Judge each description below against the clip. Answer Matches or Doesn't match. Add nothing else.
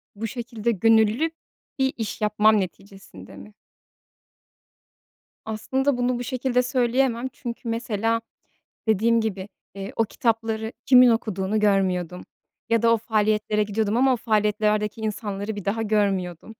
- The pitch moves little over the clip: Matches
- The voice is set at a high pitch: Matches